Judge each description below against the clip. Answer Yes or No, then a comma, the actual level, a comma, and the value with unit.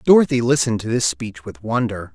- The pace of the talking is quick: No, average, 195 wpm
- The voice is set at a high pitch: No, low, 115 Hz